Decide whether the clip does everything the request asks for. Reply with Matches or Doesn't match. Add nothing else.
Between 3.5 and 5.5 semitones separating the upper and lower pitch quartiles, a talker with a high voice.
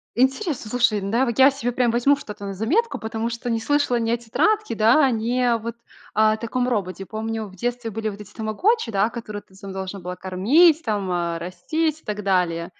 Matches